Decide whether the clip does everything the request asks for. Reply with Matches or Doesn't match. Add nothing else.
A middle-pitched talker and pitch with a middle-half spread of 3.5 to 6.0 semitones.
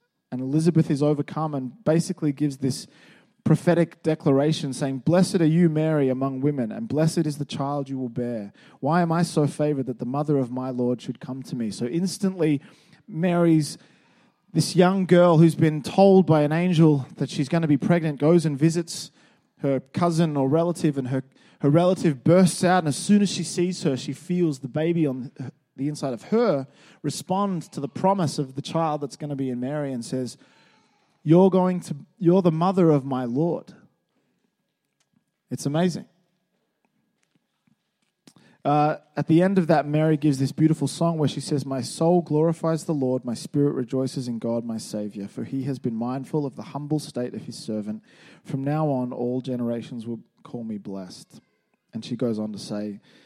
Matches